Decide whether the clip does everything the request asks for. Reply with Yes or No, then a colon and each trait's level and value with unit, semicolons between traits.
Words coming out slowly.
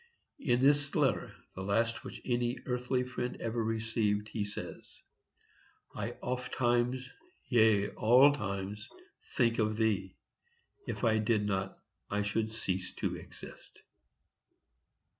Yes: slow, 115 wpm